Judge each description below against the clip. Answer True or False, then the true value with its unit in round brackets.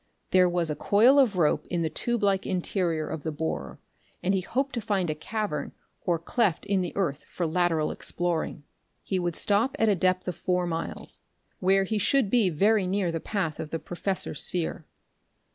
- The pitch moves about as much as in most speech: True (3.7 semitones)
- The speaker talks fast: False (195 wpm)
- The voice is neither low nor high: True (180 Hz)